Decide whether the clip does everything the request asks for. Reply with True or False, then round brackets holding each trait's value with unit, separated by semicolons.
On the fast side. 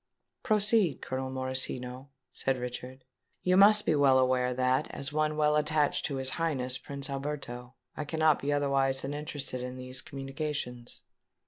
False (150 wpm)